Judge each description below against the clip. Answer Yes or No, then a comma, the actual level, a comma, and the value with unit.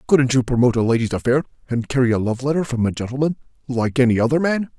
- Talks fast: Yes, fast, 225 wpm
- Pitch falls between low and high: No, low, 130 Hz